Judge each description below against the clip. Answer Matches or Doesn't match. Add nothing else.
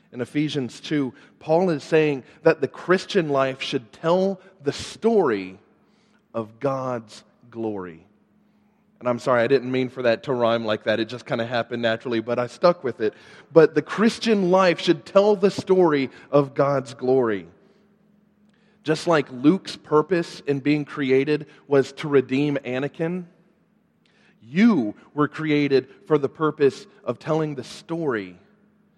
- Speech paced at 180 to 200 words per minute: Doesn't match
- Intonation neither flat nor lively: Doesn't match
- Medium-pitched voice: Matches